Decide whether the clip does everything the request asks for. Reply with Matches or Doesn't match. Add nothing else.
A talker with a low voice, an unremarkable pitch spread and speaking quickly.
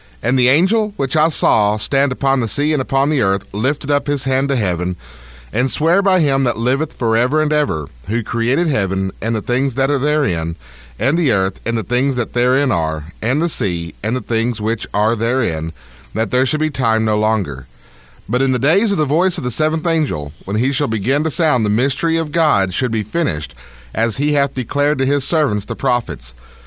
Doesn't match